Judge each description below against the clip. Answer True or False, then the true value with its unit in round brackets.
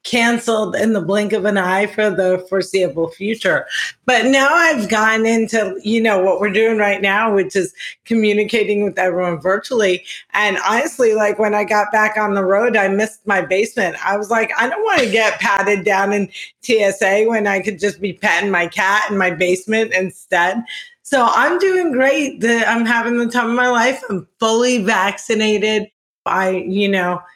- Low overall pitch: False (210 Hz)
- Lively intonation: False (2.7 semitones)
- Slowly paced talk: False (185 wpm)